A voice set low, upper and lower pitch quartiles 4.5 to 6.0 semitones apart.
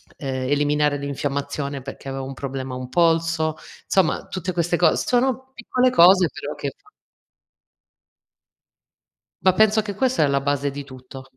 No: medium, 150 Hz; wide, 5.4 semitones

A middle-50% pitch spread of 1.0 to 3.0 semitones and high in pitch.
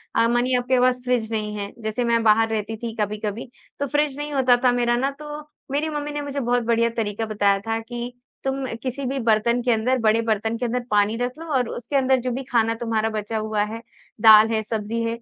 Yes: narrow, 2.6 semitones; high, 235 Hz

